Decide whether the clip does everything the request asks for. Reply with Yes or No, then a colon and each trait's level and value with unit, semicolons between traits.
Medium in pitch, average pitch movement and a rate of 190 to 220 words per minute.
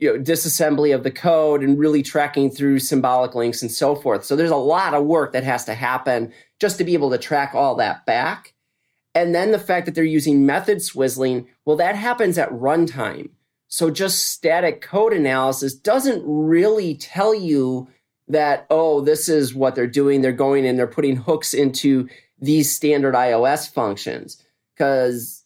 No: medium, 145 Hz; average, 3.8 semitones; average, 180 wpm